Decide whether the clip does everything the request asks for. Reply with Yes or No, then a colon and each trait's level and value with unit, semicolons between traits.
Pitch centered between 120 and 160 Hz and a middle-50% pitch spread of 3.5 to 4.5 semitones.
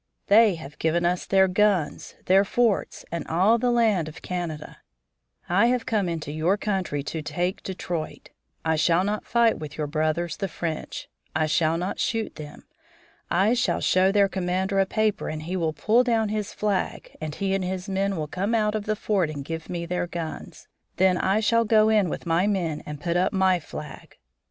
No: medium, 185 Hz; average, 4.2 semitones